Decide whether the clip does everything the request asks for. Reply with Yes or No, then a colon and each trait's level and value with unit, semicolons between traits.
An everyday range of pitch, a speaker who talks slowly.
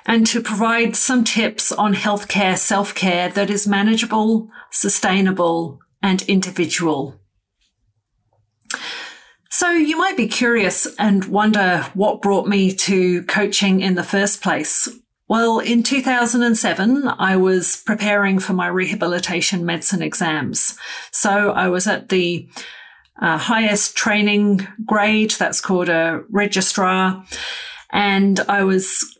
Yes: average, 3.0 semitones; slow, 120 wpm